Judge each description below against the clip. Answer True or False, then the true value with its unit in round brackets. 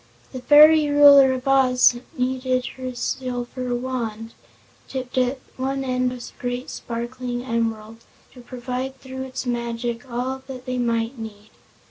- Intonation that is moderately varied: False (1.5 semitones)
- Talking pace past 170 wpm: False (145 wpm)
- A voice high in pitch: True (250 Hz)